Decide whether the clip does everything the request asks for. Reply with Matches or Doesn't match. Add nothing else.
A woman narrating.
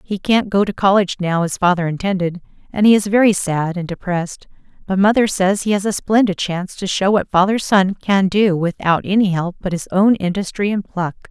Matches